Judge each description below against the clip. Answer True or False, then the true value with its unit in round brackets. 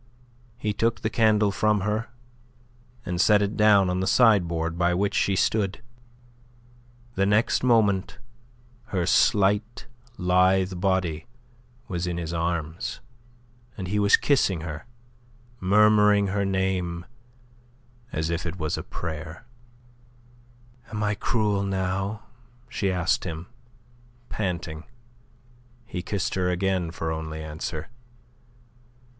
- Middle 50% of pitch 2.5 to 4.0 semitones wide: True (3.3 semitones)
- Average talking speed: False (115 wpm)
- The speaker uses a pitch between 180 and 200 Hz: False (95 Hz)